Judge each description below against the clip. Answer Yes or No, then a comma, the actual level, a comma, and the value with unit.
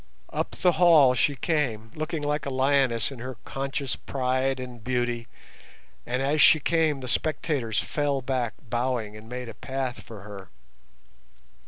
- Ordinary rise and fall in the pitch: Yes, average, 3.1 semitones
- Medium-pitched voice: No, low, 130 Hz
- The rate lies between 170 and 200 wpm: No, average, 155 wpm